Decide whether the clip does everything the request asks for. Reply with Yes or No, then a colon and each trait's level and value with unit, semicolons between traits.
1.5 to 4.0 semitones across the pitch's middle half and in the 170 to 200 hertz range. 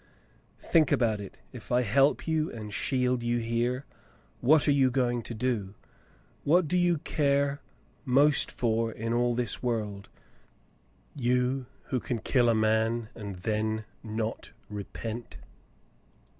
No: average, 3.3 semitones; low, 120 Hz